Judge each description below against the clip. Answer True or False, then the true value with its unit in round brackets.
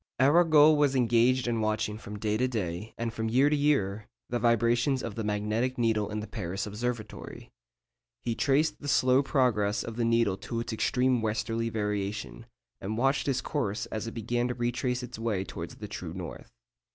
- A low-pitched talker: True (115 Hz)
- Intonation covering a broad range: False (3.0 semitones)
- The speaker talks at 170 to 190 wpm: True (185 wpm)